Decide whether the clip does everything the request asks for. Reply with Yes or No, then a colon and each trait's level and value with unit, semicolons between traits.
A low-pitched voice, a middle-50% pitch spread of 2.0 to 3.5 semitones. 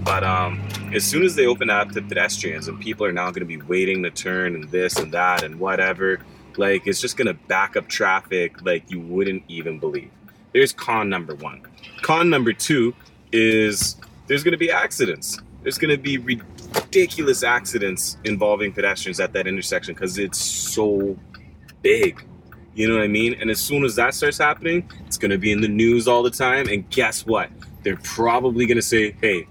No: low, 110 Hz; average, 4.5 semitones